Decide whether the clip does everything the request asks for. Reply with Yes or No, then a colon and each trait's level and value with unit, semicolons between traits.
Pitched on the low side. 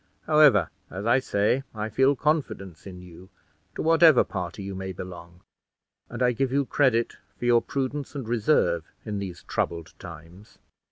Yes: low, 110 Hz